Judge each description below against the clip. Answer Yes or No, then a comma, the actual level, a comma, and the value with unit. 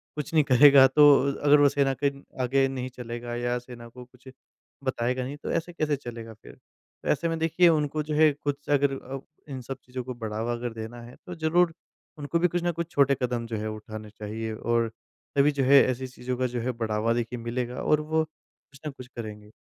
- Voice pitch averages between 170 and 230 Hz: No, low, 130 Hz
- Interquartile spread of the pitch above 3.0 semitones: Yes, average, 3.7 semitones